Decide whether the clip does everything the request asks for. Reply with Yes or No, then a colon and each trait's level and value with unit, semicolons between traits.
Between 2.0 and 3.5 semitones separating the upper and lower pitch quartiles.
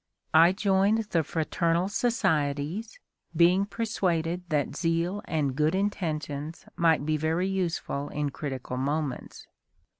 No: average, 4.1 semitones